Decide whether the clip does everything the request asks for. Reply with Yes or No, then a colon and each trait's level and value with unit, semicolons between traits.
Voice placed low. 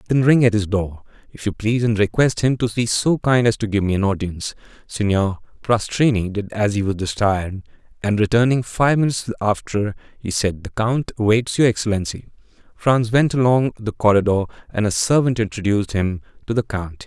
Yes: low, 110 Hz